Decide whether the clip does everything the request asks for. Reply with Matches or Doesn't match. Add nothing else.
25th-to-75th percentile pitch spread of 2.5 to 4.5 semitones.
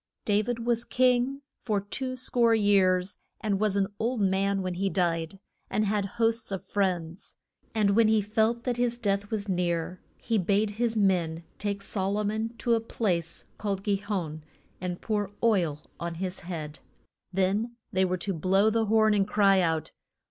Matches